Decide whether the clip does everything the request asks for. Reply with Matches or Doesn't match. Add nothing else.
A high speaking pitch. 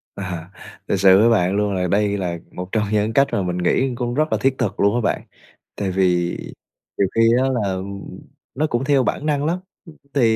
Doesn't match